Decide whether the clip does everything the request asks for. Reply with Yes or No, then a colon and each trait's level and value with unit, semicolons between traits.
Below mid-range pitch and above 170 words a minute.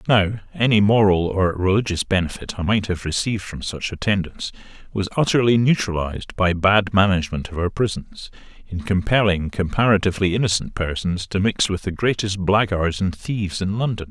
No: low, 100 Hz; average, 155 wpm